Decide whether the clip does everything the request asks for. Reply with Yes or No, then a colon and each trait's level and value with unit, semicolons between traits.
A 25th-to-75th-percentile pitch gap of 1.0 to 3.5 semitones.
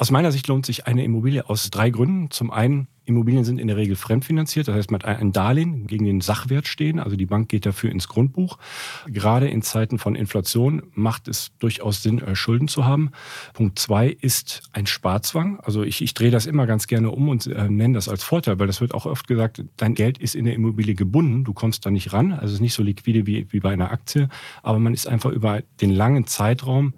No: average, 3.9 semitones